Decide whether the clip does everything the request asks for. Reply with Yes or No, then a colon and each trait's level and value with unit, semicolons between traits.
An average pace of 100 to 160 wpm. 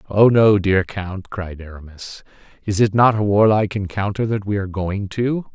No: average, 185 wpm